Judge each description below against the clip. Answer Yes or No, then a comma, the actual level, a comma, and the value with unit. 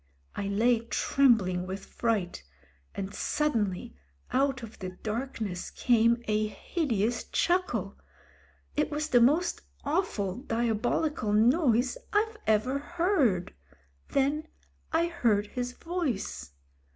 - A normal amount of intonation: No, wide, 6.0 semitones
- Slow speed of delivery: Yes, slow, 110 wpm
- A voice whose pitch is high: Yes, high, 240 Hz